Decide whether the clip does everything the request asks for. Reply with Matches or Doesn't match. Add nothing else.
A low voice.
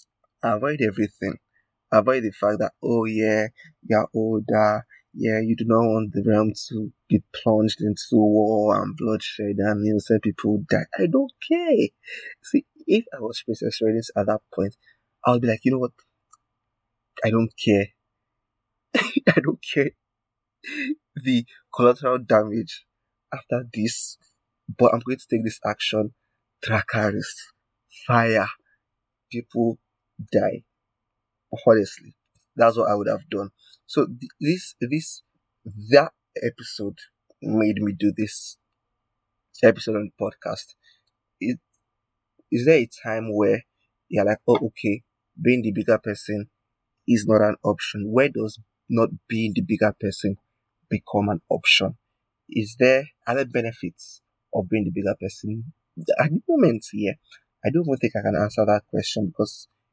Matches